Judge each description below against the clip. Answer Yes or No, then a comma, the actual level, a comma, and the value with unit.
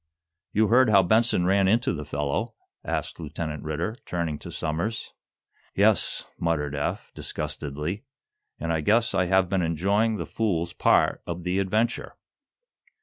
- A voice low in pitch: Yes, very low, 90 Hz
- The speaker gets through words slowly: No, average, 145 wpm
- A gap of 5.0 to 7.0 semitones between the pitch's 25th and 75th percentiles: Yes, average, 5.3 semitones